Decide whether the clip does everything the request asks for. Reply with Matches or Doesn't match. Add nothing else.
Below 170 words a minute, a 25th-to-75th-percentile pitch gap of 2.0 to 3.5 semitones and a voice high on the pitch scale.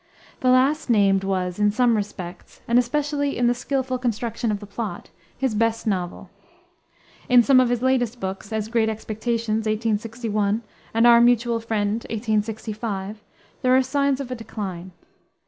Matches